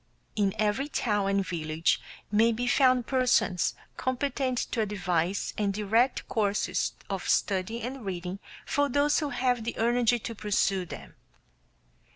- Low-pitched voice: No, high, 220 Hz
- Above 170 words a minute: No, average, 140 wpm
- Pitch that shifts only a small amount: No, average, 4.2 semitones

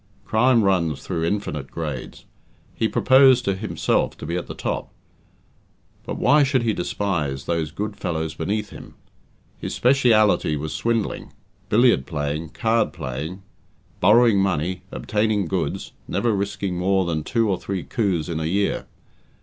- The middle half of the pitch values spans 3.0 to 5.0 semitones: No, wide, 5.5 semitones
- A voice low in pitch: Yes, very low, 95 Hz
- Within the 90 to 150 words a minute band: Yes, average, 145 wpm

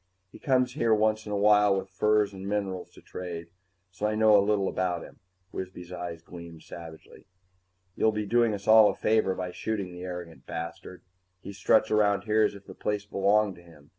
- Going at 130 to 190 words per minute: No, average, 200 wpm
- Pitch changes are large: No, average, 3.1 semitones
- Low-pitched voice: Yes, low, 100 Hz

